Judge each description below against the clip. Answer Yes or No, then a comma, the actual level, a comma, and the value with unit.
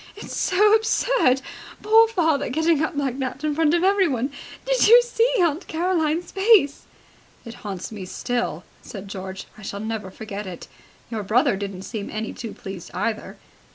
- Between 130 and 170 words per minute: Yes, average, 165 wpm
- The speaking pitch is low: No, very high, 275 Hz